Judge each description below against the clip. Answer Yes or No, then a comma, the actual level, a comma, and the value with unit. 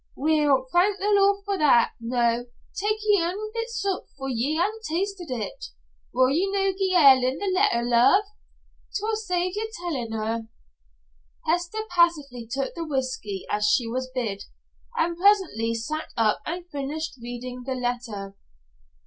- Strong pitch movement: Yes, wide, 8.0 semitones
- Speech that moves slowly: No, average, 155 wpm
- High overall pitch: Yes, very high, 300 Hz